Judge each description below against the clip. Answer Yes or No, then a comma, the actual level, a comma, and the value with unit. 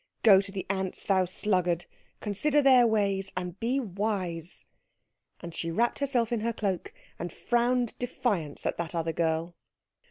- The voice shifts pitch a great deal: No, average, 5.0 semitones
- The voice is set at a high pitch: Yes, high, 195 Hz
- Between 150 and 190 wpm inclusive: Yes, average, 155 wpm